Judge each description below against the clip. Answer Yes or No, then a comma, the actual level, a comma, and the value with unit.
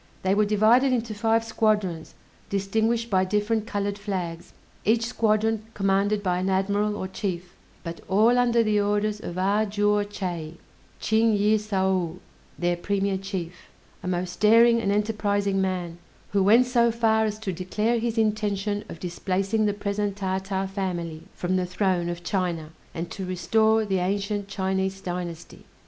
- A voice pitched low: No, high, 200 Hz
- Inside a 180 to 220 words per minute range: No, average, 155 wpm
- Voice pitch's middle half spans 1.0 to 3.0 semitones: Yes, narrow, 2.5 semitones